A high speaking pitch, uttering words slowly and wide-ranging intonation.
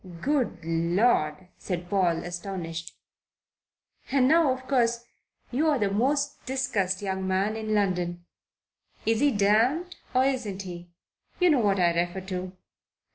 Yes: high, 200 Hz; slow, 130 wpm; wide, 6.2 semitones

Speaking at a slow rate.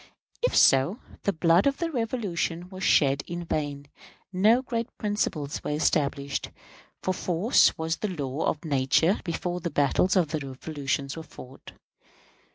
No: average, 150 wpm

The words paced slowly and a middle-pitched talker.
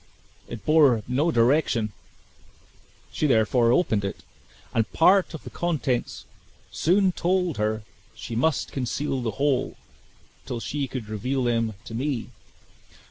No: slow, 130 wpm; low, 130 Hz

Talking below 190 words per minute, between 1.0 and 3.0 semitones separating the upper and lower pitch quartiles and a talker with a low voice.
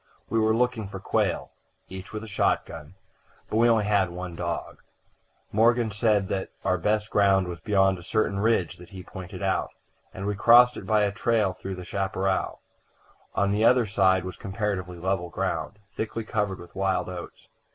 Yes: average, 180 wpm; average, 2.7 semitones; low, 100 Hz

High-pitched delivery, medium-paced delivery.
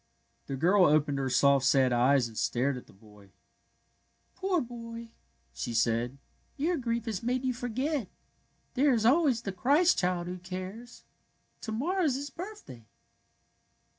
Yes: high, 215 Hz; average, 165 wpm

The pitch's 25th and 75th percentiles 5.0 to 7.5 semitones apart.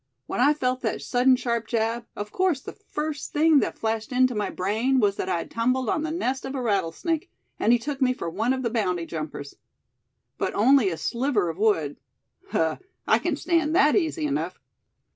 Yes: wide, 5.4 semitones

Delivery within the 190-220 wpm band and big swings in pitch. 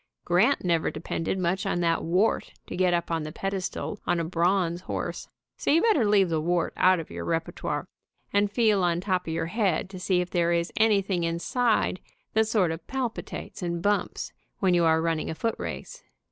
No: average, 195 wpm; average, 3.3 semitones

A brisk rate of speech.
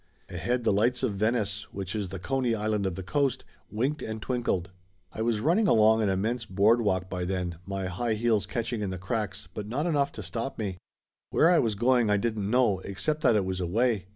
Yes: fast, 210 wpm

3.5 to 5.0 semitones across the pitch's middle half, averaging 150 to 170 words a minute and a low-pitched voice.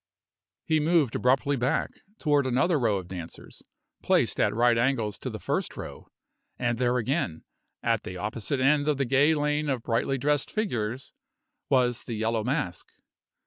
Yes: average, 4.1 semitones; average, 160 wpm; low, 125 Hz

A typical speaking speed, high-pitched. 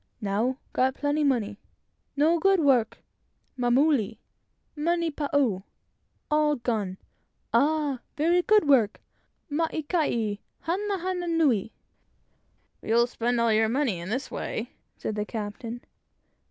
No: slow, 115 wpm; very high, 265 Hz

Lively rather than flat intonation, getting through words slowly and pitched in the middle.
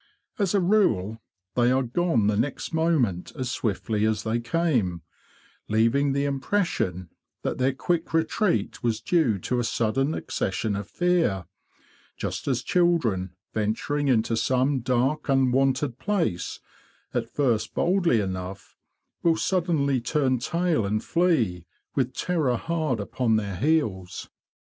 No: wide, 6.7 semitones; slow, 130 wpm; low, 130 Hz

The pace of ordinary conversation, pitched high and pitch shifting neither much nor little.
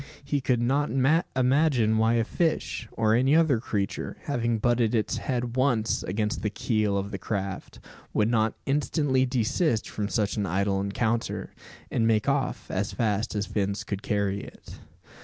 No: average, 160 wpm; low, 115 Hz; average, 3.7 semitones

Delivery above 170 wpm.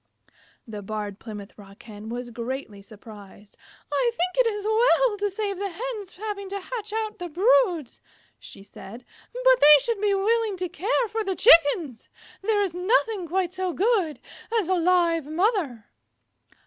No: average, 160 wpm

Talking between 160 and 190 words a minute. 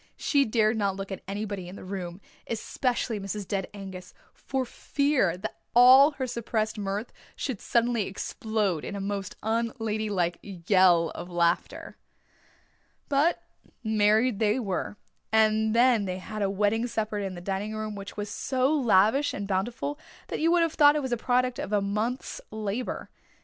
Yes: average, 165 wpm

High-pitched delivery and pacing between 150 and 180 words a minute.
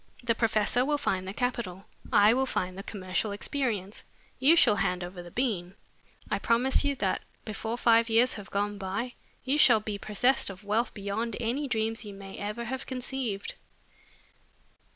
Yes: high, 220 Hz; average, 170 wpm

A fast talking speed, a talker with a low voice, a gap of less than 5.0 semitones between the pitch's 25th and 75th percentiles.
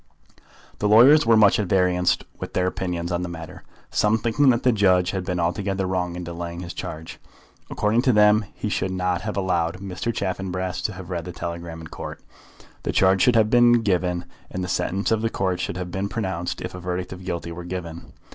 Yes: fast, 215 wpm; very low, 95 Hz; average, 2.9 semitones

